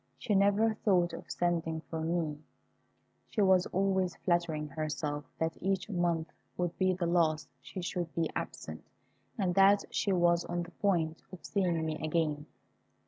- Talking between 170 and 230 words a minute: No, average, 155 wpm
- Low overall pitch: No, medium, 175 Hz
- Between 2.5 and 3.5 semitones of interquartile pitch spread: Yes, average, 2.8 semitones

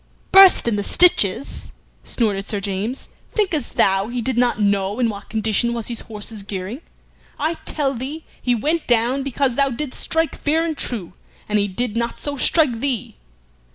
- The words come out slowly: No, average, 175 wpm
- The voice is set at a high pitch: Yes, high, 240 Hz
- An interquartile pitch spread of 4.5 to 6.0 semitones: Yes, average, 5.1 semitones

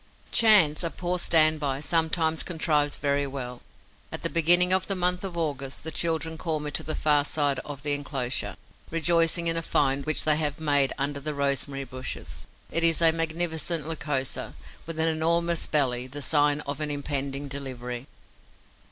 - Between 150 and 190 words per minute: Yes, average, 175 wpm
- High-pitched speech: No, medium, 150 Hz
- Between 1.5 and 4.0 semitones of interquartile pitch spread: Yes, average, 2.7 semitones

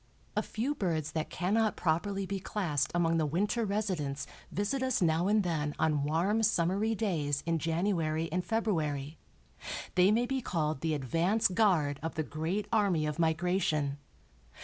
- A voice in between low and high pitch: Yes, medium, 170 Hz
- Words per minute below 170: Yes, average, 155 wpm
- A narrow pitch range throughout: No, average, 4.8 semitones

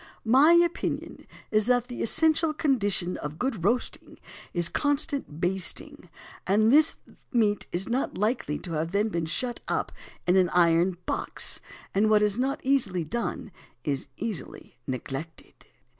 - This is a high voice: Yes, high, 210 Hz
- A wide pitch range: Yes, wide, 6.6 semitones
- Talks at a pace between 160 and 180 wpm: No, average, 145 wpm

